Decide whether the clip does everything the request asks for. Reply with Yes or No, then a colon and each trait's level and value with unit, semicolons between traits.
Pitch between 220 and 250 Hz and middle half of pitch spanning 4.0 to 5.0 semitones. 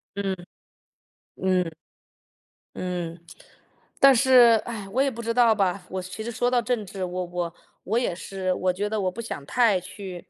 No: high, 195 Hz; average, 4.3 semitones